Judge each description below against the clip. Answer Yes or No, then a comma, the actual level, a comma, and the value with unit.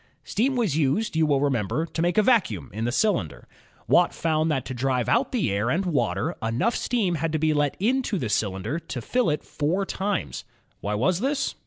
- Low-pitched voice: No, medium, 155 Hz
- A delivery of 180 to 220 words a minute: Yes, fast, 205 wpm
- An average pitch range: No, wide, 8.3 semitones